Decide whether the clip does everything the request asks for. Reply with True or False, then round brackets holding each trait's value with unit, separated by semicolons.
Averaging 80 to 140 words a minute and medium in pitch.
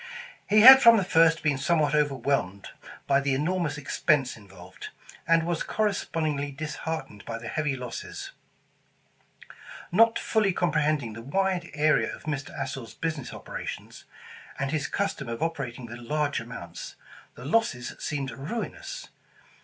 True (135 wpm; 150 Hz)